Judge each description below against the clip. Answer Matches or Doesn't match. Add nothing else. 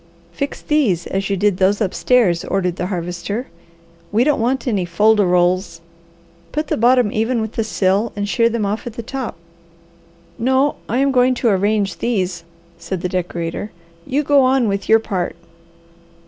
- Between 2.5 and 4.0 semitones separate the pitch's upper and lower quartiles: Doesn't match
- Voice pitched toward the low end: Doesn't match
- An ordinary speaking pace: Matches